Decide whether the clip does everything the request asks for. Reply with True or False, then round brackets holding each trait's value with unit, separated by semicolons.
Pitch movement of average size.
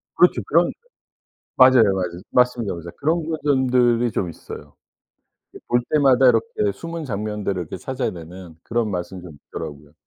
False (6.7 semitones)